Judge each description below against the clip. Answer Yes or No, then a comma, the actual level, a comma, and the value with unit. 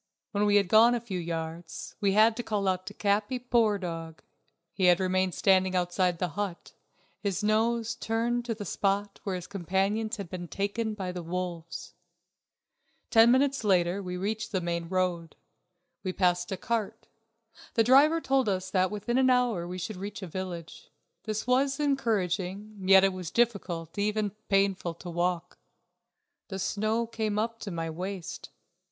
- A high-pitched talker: Yes, high, 195 Hz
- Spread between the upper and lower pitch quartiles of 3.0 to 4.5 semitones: Yes, average, 3.5 semitones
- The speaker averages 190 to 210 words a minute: No, average, 165 wpm